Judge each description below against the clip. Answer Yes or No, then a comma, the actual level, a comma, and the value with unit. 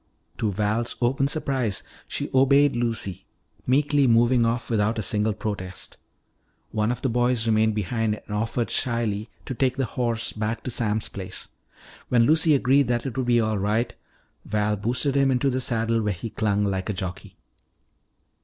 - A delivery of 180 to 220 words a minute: No, average, 170 wpm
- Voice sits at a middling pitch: No, low, 115 Hz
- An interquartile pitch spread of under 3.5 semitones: Yes, average, 3.0 semitones